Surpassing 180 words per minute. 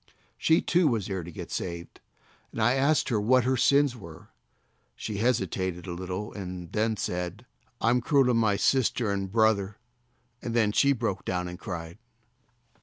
No: average, 165 wpm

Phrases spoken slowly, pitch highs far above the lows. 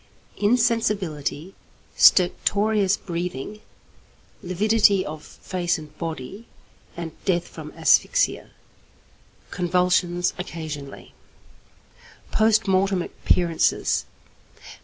No: slow, 70 wpm; average, 3.5 semitones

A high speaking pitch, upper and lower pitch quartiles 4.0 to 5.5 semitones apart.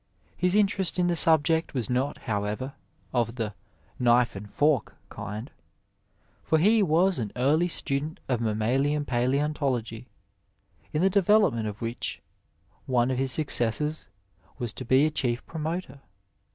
No: low, 135 Hz; average, 5.1 semitones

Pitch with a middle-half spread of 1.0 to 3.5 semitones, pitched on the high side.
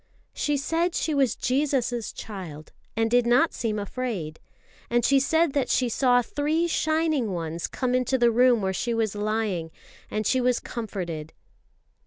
No: average, 4.3 semitones; high, 240 Hz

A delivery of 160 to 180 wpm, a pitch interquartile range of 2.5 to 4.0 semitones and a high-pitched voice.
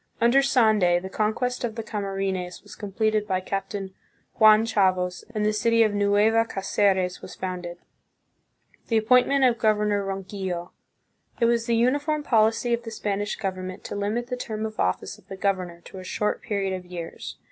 Yes: average, 170 wpm; average, 3.2 semitones; high, 210 Hz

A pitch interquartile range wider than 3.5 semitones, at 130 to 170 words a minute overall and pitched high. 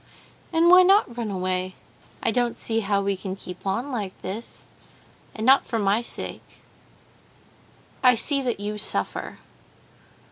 Yes: average, 4.3 semitones; average, 140 wpm; high, 220 Hz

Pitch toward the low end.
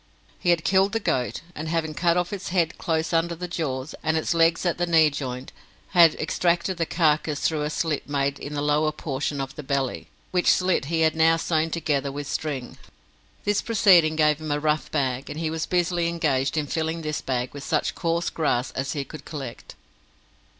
No: medium, 155 Hz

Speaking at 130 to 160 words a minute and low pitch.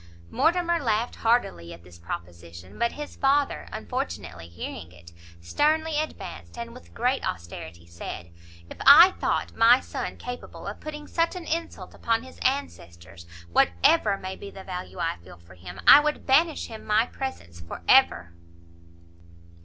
No: average, 155 wpm; high, 210 Hz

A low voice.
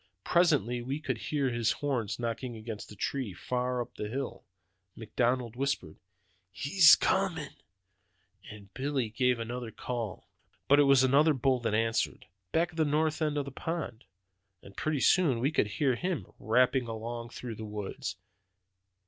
Yes: low, 125 Hz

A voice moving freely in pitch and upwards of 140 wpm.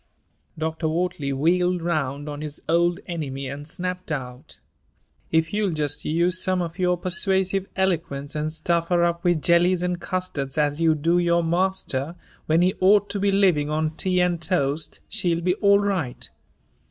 No: average, 2.9 semitones; average, 165 wpm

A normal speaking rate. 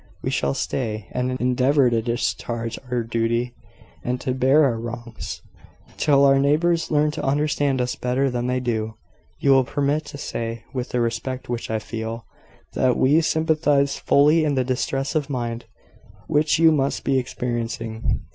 Yes: average, 165 wpm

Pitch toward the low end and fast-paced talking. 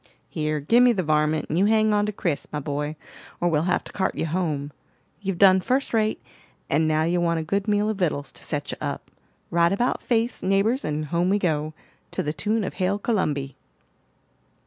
No: medium, 180 Hz; fast, 210 wpm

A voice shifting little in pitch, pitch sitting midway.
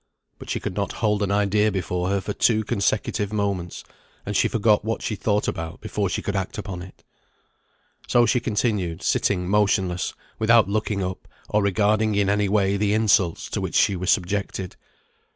No: narrow, 1.9 semitones; low, 100 Hz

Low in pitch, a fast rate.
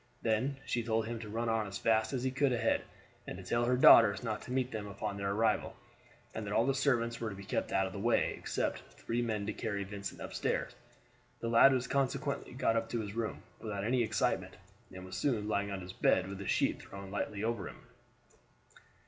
Yes: low, 110 Hz; fast, 225 wpm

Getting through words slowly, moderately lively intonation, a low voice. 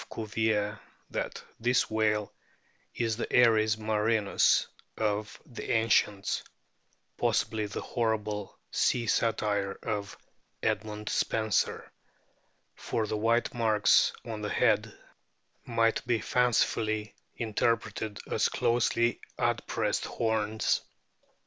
No: slow, 100 wpm; narrow, 1.4 semitones; low, 110 Hz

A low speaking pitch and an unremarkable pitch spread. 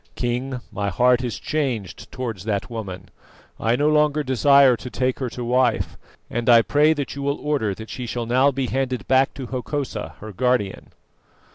Yes: low, 125 Hz; average, 3.0 semitones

